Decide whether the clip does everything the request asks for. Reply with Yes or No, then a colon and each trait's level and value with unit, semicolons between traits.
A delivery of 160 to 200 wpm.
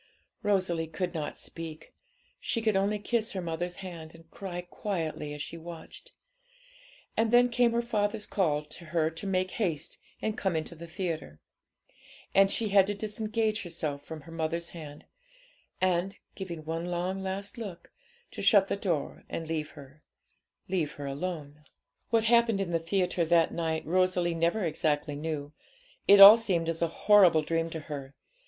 Yes: average, 165 wpm